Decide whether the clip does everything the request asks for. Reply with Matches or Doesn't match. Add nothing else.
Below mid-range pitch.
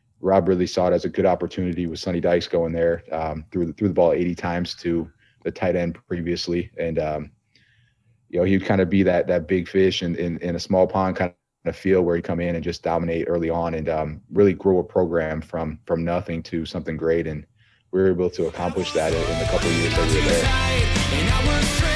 Matches